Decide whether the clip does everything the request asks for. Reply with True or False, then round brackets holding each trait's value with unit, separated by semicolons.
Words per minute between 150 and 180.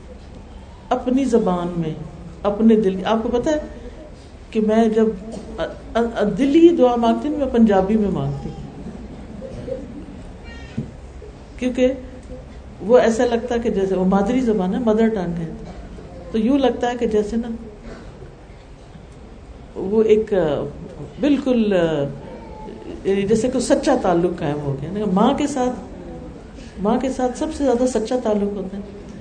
False (135 wpm)